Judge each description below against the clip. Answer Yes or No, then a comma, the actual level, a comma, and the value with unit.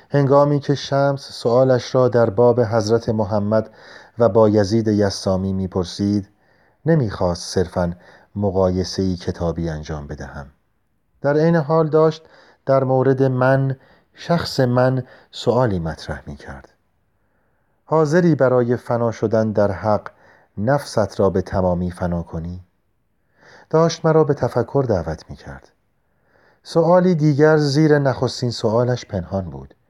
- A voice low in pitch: Yes, low, 115 Hz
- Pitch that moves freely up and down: Yes, wide, 6.3 semitones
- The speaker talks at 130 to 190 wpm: No, average, 120 wpm